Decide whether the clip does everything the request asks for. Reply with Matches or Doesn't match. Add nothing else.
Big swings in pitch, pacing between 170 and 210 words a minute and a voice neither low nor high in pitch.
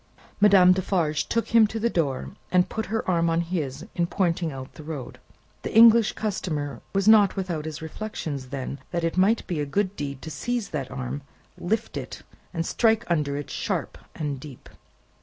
Matches